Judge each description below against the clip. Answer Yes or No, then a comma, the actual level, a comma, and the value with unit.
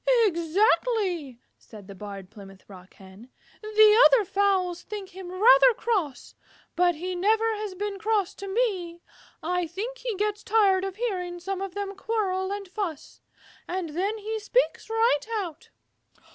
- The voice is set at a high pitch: Yes, very high, 385 Hz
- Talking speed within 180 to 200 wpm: No, average, 150 wpm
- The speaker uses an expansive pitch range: No, average, 3.7 semitones